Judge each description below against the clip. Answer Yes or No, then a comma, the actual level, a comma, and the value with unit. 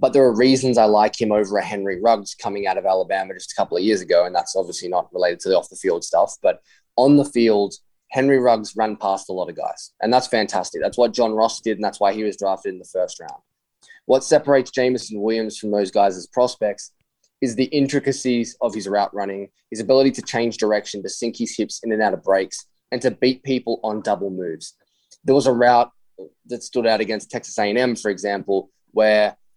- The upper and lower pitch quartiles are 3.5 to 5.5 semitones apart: Yes, average, 3.8 semitones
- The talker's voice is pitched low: Yes, low, 110 Hz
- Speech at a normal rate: No, fast, 220 wpm